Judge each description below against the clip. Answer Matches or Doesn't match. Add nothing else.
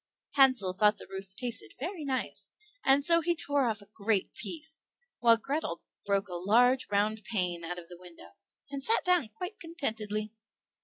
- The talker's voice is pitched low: Doesn't match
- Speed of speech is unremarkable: Matches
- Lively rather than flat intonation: Matches